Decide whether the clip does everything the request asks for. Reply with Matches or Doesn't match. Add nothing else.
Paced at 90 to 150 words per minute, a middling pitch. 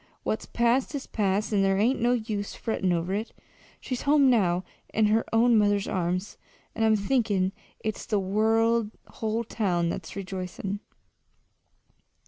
Doesn't match